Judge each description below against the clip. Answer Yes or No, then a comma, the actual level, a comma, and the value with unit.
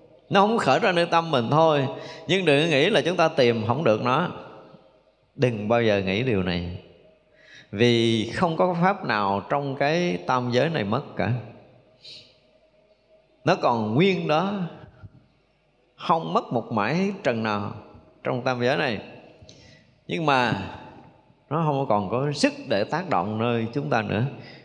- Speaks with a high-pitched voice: No, low, 125 Hz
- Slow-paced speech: Yes, slow, 155 wpm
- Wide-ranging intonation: Yes, wide, 5.7 semitones